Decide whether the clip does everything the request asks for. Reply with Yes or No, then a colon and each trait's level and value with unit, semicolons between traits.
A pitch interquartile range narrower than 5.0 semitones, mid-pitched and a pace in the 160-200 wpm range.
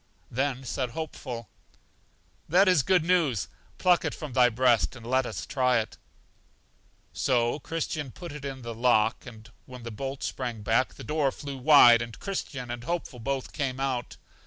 No: average, 3.5 semitones; low, 130 Hz; average, 165 wpm